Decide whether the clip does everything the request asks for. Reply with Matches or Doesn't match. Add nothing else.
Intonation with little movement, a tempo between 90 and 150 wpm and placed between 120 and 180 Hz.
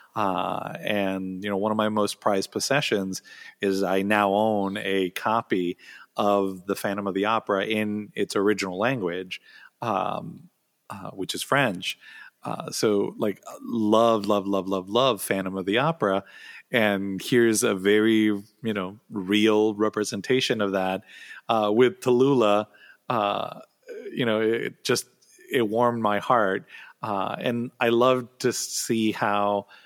Doesn't match